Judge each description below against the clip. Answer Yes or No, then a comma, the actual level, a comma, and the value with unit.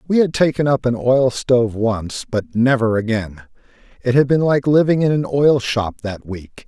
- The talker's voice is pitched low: Yes, low, 125 Hz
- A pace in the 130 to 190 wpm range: No, average, 200 wpm